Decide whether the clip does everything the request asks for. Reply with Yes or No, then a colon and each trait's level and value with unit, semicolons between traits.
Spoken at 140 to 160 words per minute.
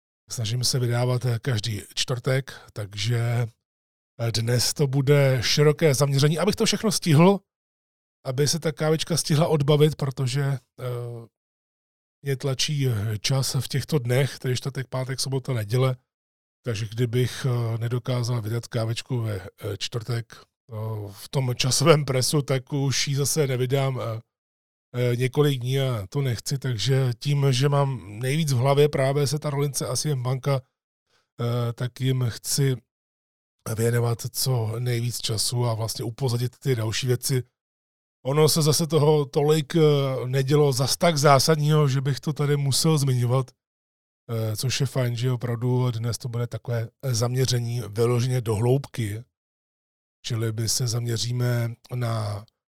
No: average, 130 wpm